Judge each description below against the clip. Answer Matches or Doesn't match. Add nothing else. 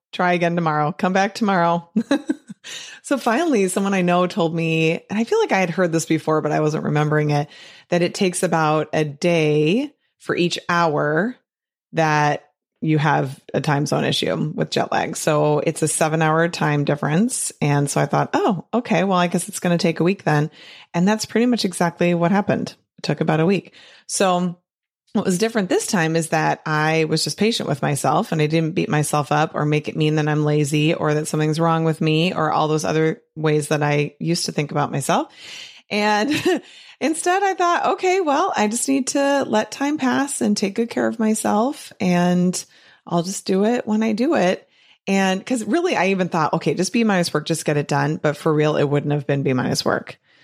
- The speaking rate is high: Matches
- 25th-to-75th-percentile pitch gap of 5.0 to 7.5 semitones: Matches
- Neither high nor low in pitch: Matches